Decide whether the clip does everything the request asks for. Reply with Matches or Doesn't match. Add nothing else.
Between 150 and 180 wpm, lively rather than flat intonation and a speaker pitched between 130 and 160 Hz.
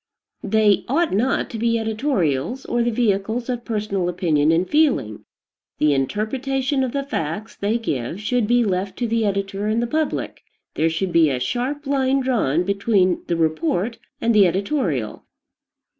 Doesn't match